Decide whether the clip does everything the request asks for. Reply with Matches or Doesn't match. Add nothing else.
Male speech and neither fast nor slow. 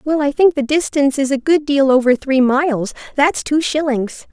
Doesn't match